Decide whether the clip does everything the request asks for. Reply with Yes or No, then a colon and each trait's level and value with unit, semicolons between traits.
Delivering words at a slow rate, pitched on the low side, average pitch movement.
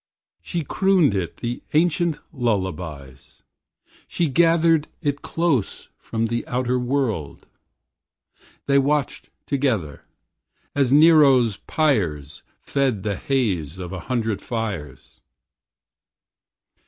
No: slow, 95 wpm; low, 125 Hz; wide, 7.2 semitones